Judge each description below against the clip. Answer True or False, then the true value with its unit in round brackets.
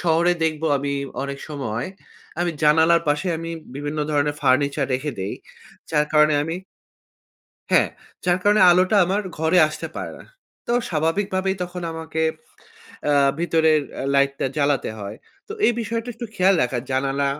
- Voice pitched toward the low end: False (155 Hz)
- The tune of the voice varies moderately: True (3.8 semitones)